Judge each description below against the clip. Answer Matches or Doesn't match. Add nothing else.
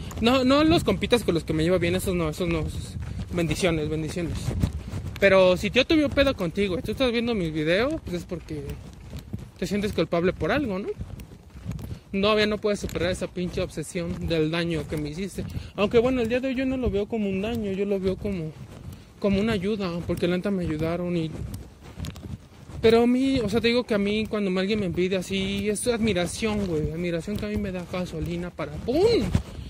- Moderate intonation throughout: Matches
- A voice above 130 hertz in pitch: Matches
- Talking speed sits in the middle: Doesn't match